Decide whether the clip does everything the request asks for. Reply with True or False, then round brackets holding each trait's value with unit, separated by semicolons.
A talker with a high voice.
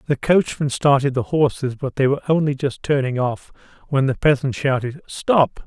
False (140 Hz)